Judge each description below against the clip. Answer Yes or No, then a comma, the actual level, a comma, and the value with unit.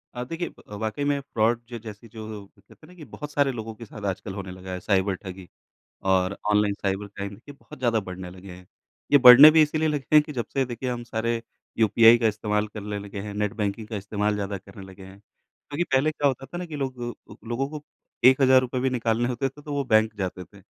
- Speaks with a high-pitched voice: No, low, 110 Hz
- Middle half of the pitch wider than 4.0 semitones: Yes, average, 4.7 semitones